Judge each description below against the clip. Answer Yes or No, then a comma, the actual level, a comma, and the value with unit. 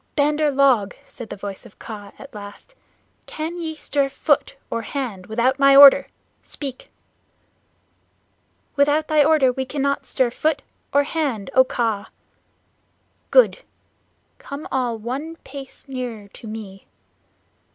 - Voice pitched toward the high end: Yes, very high, 270 Hz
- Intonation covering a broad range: No, average, 4.3 semitones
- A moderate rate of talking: No, slow, 130 wpm